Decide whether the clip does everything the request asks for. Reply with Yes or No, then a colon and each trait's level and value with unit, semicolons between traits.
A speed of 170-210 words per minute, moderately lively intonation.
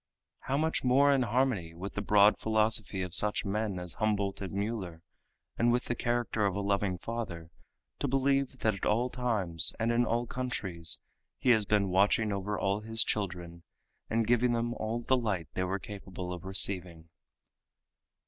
Yes: average, 175 wpm; average, 3.9 semitones